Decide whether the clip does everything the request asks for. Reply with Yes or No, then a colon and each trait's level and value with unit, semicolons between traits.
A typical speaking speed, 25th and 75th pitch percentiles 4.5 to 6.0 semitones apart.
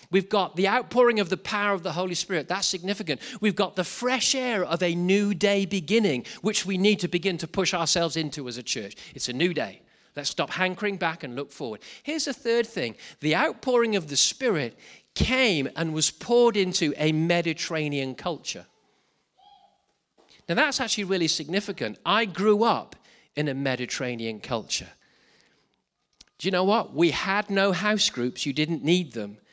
Yes: average, 180 wpm; average, 4.8 semitones